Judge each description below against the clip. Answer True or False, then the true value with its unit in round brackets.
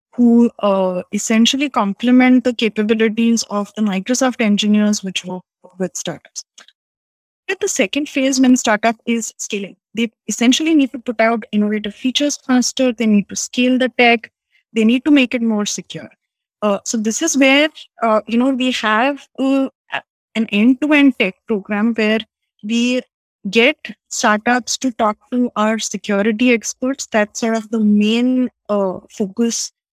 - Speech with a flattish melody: False (3.3 semitones)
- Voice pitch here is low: False (230 Hz)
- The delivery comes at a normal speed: True (150 wpm)